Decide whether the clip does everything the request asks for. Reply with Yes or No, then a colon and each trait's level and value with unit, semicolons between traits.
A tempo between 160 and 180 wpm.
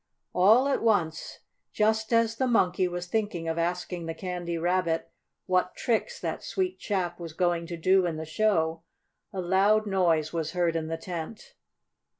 Yes: average, 165 wpm